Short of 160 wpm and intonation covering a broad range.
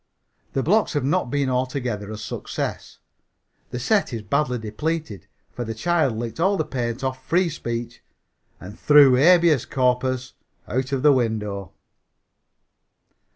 No: average, 140 wpm; average, 4.2 semitones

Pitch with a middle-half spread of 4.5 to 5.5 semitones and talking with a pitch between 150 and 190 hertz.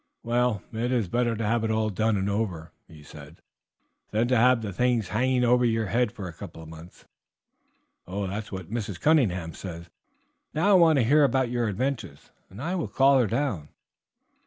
No: average, 4.8 semitones; low, 110 Hz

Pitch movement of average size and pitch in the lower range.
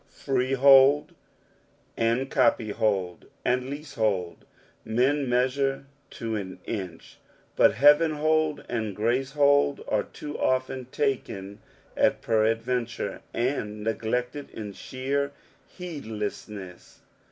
Yes: average, 4.3 semitones; low, 125 Hz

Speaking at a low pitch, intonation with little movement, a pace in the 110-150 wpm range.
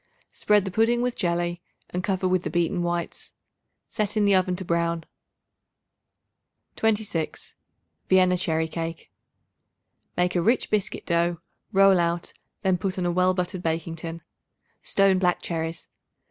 No: medium, 180 Hz; narrow, 2.3 semitones; average, 145 wpm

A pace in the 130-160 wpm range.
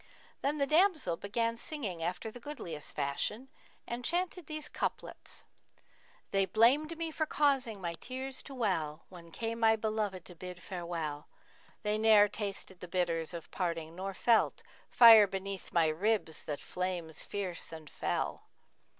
Yes: average, 155 wpm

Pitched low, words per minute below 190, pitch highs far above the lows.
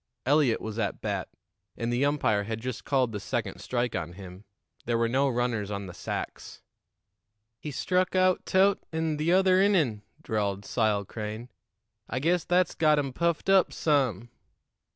Yes: low, 125 Hz; average, 160 wpm; wide, 6.9 semitones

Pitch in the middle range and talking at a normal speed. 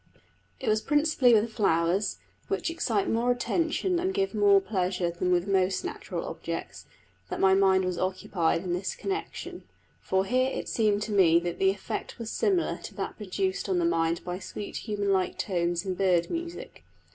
No: high, 195 Hz; average, 175 wpm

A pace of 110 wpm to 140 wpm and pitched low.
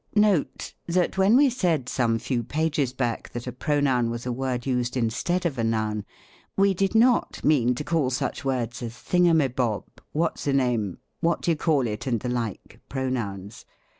No: average, 175 wpm; low, 130 Hz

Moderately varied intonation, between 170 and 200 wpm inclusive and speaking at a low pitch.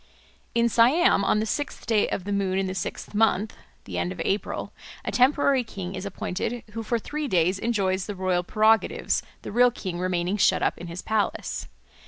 No: average, 3.7 semitones; average, 195 wpm; high, 205 Hz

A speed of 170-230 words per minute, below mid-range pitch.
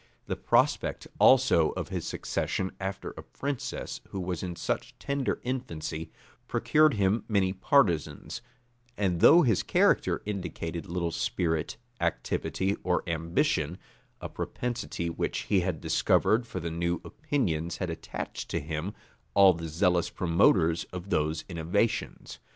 No: slow, 135 wpm; very low, 90 Hz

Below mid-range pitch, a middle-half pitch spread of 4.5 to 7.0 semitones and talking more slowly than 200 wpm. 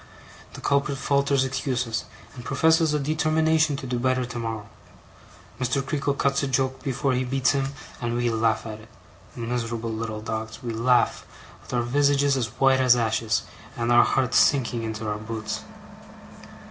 No: low, 125 Hz; average, 3.2 semitones; average, 160 wpm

